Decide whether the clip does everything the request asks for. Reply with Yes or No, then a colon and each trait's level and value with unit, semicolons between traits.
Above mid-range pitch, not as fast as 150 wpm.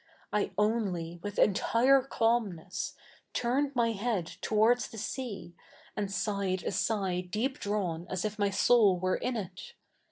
Yes: high, 210 Hz; average, 140 wpm